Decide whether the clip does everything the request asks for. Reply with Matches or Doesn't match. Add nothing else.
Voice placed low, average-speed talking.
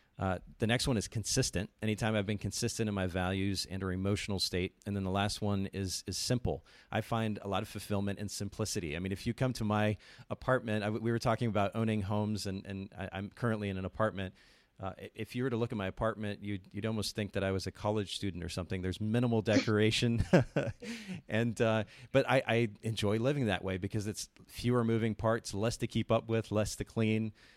Doesn't match